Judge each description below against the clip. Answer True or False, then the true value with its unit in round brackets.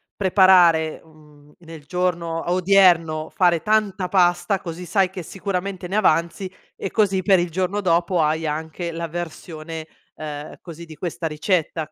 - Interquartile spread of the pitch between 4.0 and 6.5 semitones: False (2.7 semitones)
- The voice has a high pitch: False (175 Hz)